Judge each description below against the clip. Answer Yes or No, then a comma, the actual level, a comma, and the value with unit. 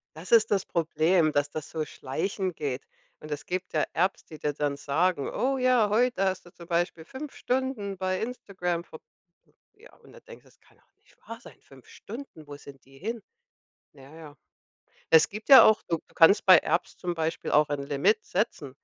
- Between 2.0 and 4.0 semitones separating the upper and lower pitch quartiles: No, wide, 5.7 semitones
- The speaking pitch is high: No, medium, 175 Hz